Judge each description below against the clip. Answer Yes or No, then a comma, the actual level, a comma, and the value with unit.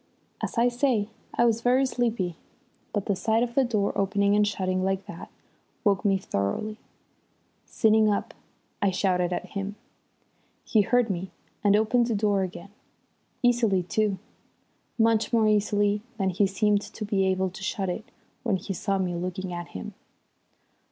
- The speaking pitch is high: Yes, high, 205 Hz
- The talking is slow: No, average, 160 wpm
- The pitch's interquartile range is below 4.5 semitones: Yes, narrow, 2.6 semitones